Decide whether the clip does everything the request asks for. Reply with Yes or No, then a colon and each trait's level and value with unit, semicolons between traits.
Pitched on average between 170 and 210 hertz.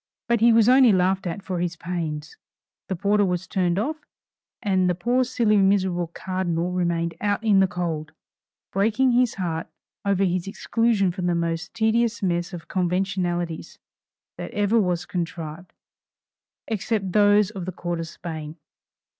Yes: medium, 185 Hz